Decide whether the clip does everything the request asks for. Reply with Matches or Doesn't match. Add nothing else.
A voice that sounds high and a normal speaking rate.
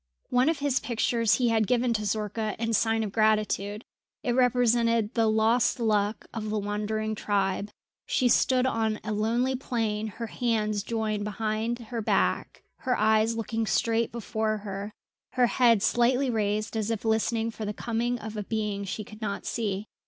Matches